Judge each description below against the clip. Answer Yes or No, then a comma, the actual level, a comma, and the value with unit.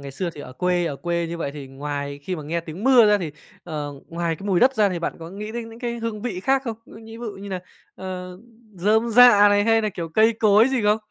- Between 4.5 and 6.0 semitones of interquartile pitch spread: Yes, average, 4.9 semitones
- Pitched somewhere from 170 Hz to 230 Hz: Yes, high, 195 Hz